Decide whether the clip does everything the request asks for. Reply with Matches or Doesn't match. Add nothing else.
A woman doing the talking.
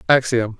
Doesn't match